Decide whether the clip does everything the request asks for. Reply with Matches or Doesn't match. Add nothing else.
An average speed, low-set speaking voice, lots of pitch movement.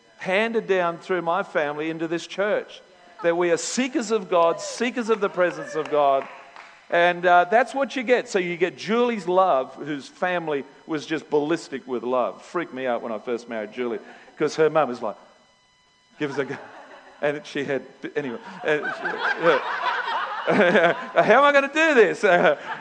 Doesn't match